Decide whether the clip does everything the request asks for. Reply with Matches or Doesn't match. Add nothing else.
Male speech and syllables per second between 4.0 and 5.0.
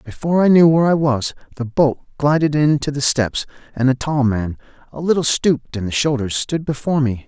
Doesn't match